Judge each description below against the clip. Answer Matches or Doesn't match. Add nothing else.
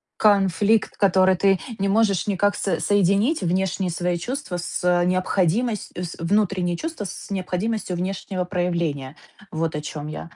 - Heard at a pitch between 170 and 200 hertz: Matches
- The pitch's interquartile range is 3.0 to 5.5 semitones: Doesn't match